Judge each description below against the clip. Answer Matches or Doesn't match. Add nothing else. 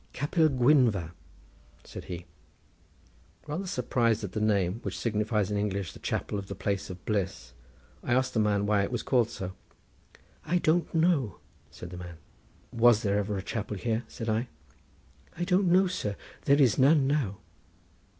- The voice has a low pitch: Matches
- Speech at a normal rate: Matches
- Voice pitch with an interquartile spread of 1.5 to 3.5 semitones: Doesn't match